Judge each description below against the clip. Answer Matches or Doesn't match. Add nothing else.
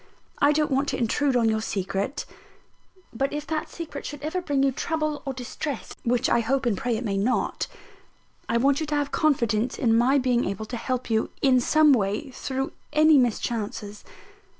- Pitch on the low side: Doesn't match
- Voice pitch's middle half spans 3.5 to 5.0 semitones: Matches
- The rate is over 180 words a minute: Matches